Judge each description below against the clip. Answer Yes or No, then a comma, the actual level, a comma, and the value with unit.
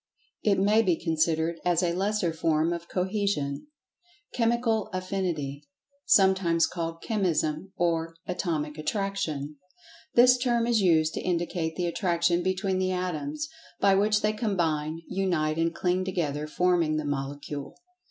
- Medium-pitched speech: Yes, medium, 175 Hz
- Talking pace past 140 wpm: No, slow, 135 wpm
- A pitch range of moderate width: Yes, average, 3.6 semitones